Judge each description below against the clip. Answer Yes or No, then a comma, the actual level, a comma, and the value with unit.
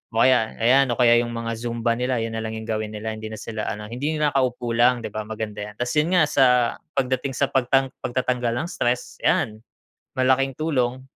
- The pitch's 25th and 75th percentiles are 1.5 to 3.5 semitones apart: Yes, average, 2.7 semitones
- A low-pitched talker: Yes, low, 120 Hz